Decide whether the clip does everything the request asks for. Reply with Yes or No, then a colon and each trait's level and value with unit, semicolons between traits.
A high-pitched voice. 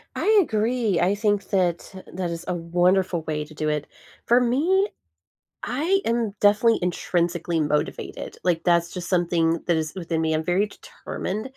No: medium, 180 Hz